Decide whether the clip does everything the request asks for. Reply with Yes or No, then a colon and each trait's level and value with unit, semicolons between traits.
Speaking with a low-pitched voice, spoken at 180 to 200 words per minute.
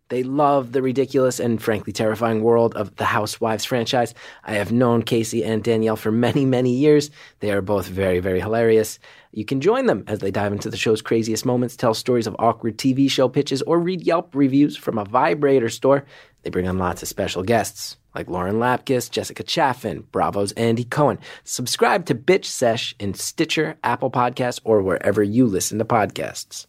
Yes: low, 115 Hz; average, 190 wpm